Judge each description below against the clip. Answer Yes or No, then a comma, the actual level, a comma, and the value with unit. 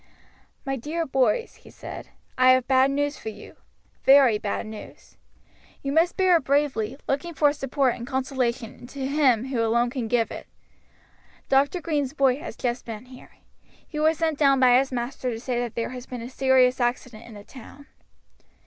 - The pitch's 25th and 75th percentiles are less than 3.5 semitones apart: Yes, average, 2.8 semitones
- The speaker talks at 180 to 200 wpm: Yes, average, 185 wpm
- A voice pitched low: No, very high, 260 Hz